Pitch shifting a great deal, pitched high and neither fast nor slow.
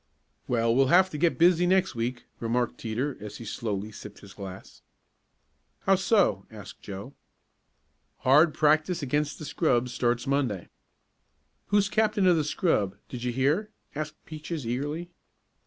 No: wide, 6.5 semitones; medium, 140 Hz; average, 145 wpm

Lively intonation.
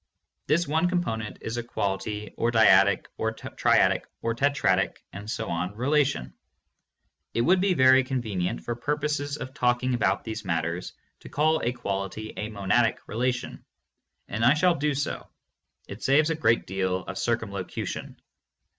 Yes: wide, 5.9 semitones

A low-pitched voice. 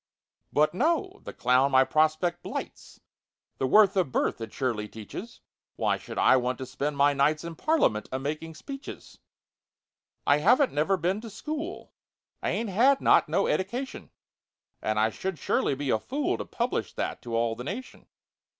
No: medium, 155 Hz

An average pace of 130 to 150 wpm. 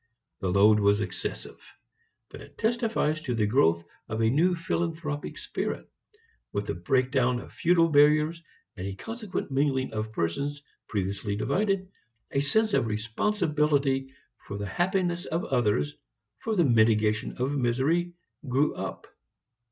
Yes: average, 140 wpm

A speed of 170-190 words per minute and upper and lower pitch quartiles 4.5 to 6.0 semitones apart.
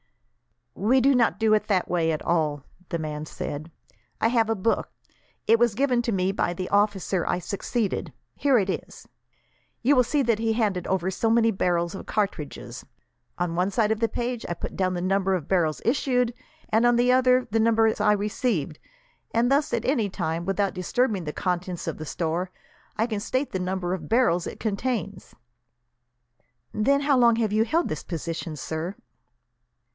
Yes: average, 185 wpm; average, 4.8 semitones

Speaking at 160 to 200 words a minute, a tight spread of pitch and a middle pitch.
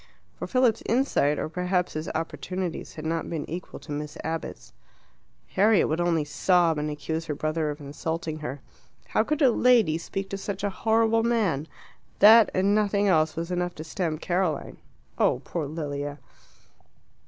No: average, 165 wpm; average, 4.5 semitones; medium, 170 Hz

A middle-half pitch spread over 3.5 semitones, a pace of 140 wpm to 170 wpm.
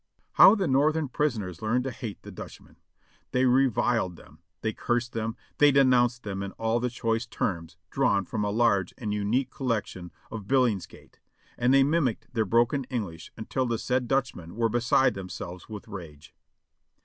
Yes: average, 4.1 semitones; average, 165 wpm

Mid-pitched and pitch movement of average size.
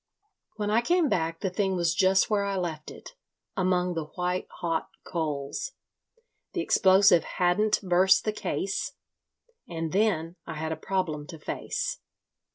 Yes: medium, 180 Hz; average, 3.4 semitones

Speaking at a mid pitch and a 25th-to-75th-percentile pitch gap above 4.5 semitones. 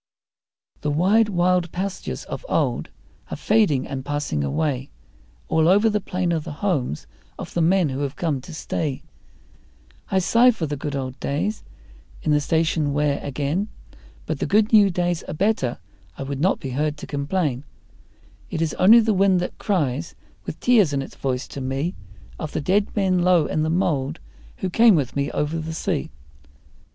Yes: medium, 160 Hz; average, 4.9 semitones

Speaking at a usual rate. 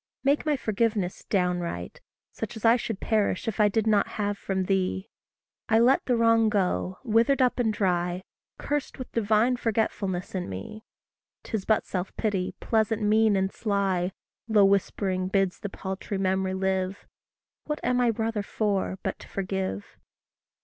Yes: average, 155 wpm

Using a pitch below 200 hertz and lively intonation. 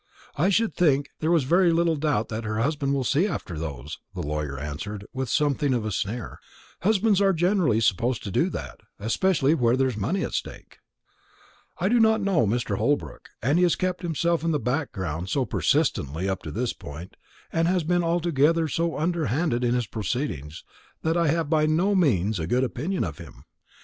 Yes: medium, 140 Hz; wide, 7.7 semitones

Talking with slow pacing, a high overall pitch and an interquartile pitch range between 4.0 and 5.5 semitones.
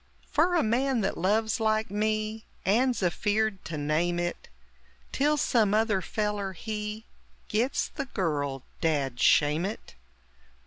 Yes: slow, 130 wpm; high, 210 Hz; average, 4.3 semitones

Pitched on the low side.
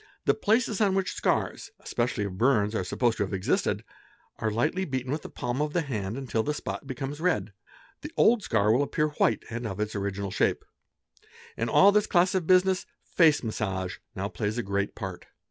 Yes: low, 120 Hz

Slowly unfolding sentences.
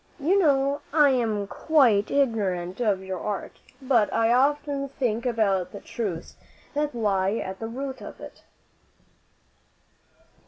Yes: slow, 130 wpm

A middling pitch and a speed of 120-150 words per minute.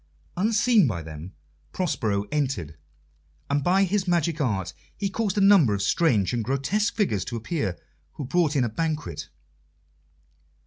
Yes: medium, 145 Hz; average, 145 wpm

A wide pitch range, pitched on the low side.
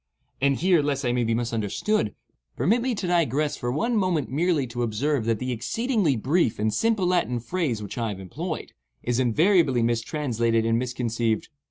Yes: wide, 7.0 semitones; low, 130 Hz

